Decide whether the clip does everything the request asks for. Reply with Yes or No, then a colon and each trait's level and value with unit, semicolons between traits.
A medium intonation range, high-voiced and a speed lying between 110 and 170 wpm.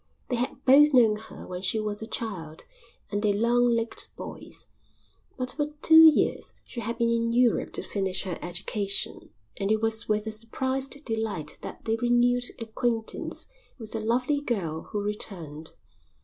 Yes: average, 3.0 semitones; high, 225 Hz; average, 165 wpm